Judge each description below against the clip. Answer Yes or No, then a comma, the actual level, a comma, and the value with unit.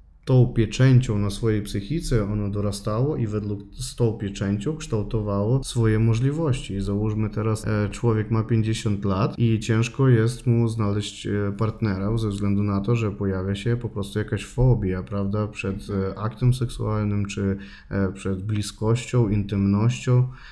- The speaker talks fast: No, average, 130 wpm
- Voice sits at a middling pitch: No, low, 110 Hz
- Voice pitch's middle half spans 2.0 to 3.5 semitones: Yes, average, 2.7 semitones